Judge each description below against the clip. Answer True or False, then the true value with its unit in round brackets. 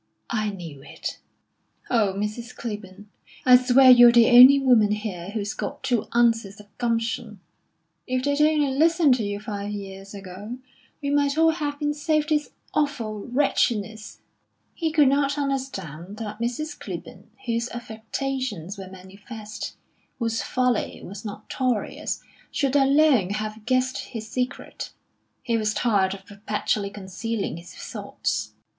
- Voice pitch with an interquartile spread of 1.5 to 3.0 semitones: False (4.5 semitones)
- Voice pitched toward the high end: True (230 Hz)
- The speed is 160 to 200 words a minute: False (140 wpm)